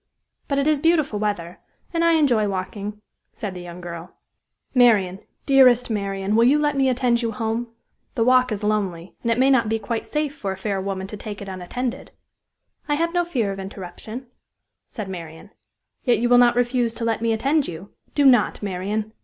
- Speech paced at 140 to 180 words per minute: No, average, 195 wpm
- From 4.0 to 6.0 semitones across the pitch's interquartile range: Yes, average, 4.5 semitones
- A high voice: Yes, high, 225 Hz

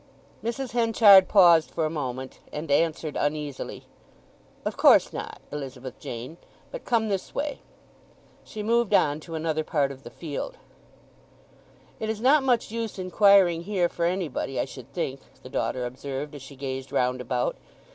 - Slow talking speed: No, average, 155 wpm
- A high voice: No, medium, 160 Hz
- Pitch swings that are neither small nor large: No, wide, 7.3 semitones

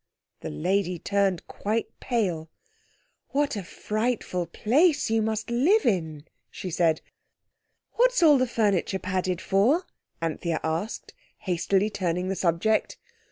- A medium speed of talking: No, slow, 120 wpm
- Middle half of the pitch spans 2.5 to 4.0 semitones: No, average, 4.8 semitones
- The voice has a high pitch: Yes, high, 200 Hz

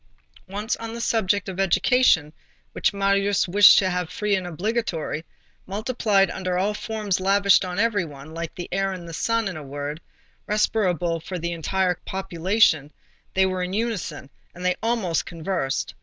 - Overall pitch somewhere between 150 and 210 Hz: Yes, high, 190 Hz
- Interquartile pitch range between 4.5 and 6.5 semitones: No, average, 3.3 semitones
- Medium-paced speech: Yes, average, 165 wpm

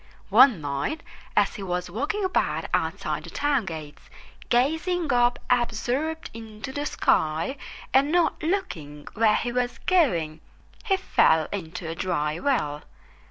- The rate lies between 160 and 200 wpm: No, slow, 135 wpm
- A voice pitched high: Yes, high, 240 Hz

